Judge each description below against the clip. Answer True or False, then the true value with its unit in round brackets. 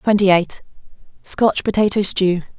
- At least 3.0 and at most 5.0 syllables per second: True (4.4 syllables/s)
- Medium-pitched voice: False (195 Hz)